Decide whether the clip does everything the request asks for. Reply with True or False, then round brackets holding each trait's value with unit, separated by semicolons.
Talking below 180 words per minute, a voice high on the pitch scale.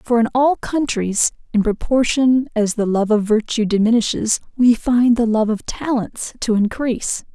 True (165 wpm; 230 Hz)